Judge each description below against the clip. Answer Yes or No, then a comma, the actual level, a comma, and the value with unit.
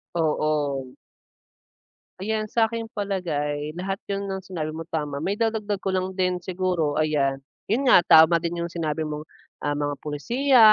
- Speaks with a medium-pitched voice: Yes, medium, 175 Hz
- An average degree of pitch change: Yes, average, 4.7 semitones